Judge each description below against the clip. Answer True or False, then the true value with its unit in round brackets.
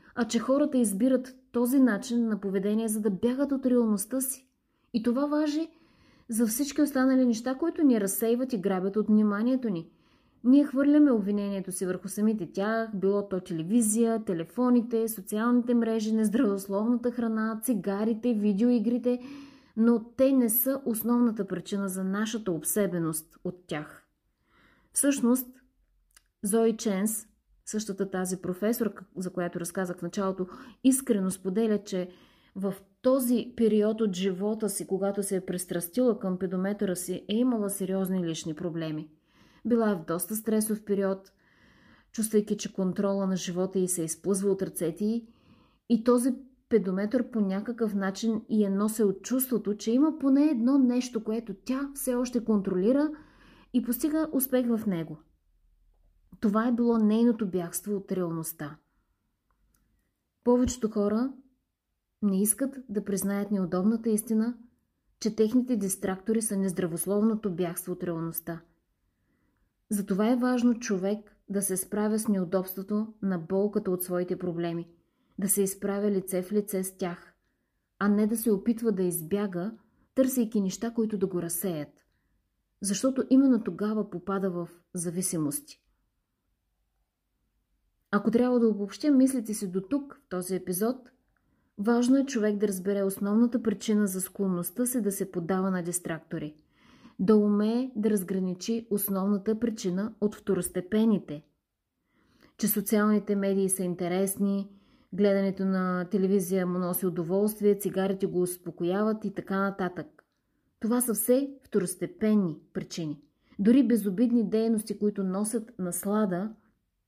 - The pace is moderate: True (130 wpm)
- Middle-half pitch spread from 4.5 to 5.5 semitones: False (3.8 semitones)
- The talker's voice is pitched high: True (210 Hz)